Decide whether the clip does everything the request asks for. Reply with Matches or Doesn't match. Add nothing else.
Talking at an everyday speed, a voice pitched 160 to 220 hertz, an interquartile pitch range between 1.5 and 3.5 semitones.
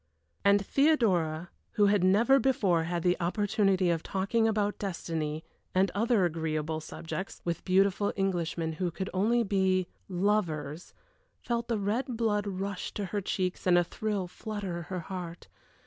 Matches